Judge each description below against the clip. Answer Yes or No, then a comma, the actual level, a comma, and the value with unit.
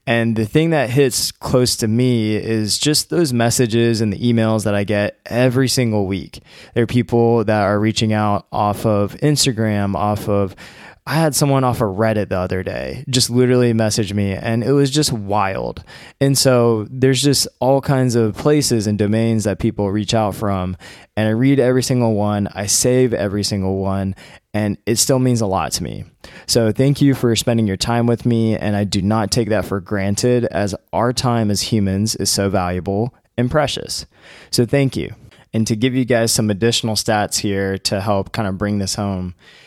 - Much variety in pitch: No, average, 3.3 semitones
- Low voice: Yes, low, 110 Hz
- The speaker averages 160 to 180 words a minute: No, average, 200 wpm